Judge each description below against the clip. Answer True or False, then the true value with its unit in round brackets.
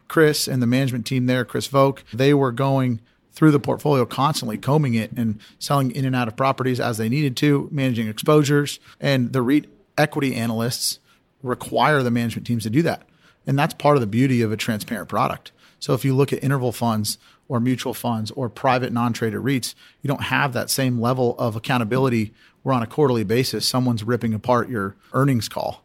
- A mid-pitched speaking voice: False (125 Hz)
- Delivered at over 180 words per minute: True (200 wpm)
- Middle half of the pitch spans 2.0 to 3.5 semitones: True (2.8 semitones)